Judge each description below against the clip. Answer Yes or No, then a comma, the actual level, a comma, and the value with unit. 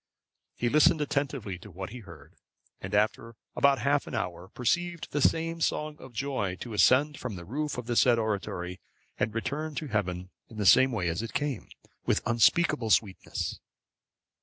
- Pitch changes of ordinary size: No, wide, 6.0 semitones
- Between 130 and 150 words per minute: No, average, 180 wpm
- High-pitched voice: No, low, 120 Hz